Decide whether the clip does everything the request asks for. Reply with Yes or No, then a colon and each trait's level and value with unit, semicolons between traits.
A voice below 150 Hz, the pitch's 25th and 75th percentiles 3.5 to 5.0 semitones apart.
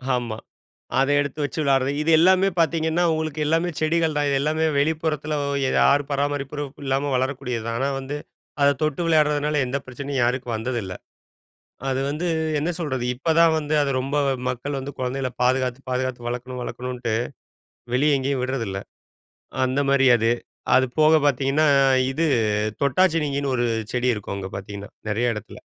No: medium, 140 Hz; average, 3.1 semitones